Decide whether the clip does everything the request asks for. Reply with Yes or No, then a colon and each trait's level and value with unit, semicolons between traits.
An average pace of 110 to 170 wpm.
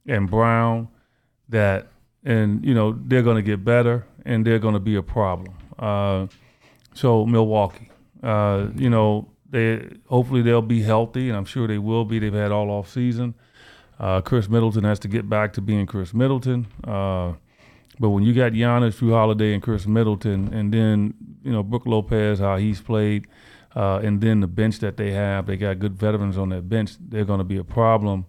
No: average, 195 wpm